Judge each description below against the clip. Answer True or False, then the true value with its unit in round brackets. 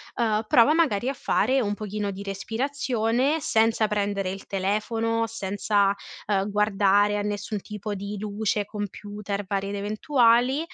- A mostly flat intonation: True (2.1 semitones)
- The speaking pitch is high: True (210 Hz)